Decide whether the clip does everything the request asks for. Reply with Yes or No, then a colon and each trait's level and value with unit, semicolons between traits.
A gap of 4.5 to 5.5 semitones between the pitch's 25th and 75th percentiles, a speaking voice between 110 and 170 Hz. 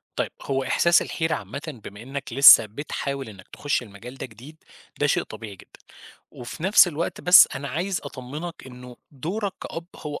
Yes: average, 4.9 semitones; medium, 140 Hz